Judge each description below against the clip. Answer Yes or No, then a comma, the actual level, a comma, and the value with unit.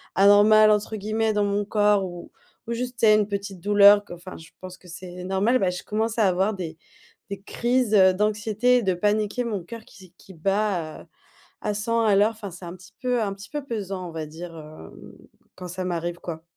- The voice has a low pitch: No, high, 200 Hz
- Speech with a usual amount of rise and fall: Yes, average, 3.0 semitones